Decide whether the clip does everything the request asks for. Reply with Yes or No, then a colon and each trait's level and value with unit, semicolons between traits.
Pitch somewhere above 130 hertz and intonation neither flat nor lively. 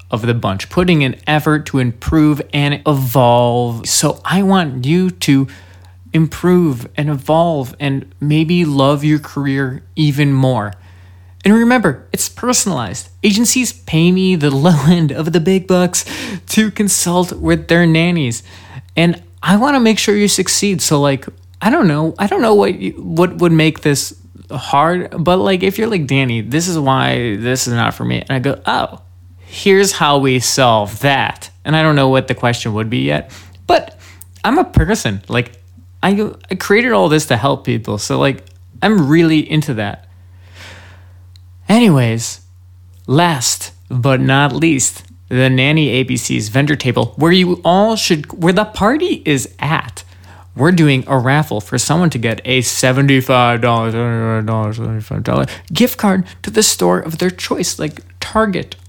No: medium, 140 Hz; wide, 7.8 semitones